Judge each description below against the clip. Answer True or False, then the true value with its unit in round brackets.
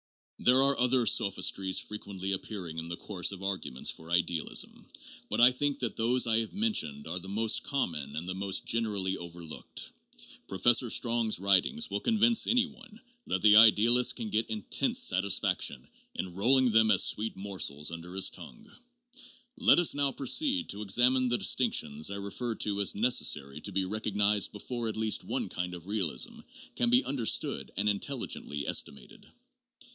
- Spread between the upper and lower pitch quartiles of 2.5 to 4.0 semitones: False (5.1 semitones)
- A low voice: True (105 Hz)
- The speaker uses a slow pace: False (165 wpm)